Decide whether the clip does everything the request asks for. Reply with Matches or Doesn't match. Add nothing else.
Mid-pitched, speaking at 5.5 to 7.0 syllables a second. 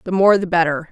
Matches